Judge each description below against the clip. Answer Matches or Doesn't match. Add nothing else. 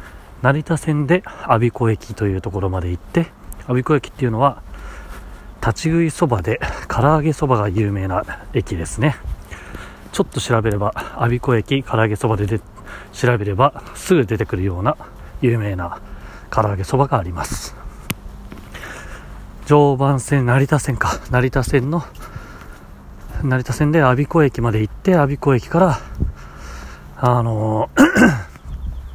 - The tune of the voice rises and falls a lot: Matches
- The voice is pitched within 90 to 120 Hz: Matches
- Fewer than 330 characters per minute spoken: Matches